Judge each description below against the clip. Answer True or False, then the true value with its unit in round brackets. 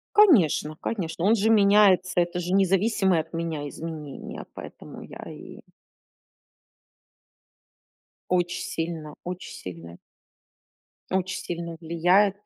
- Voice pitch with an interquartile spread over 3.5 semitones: False (3.2 semitones)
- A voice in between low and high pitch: True (175 Hz)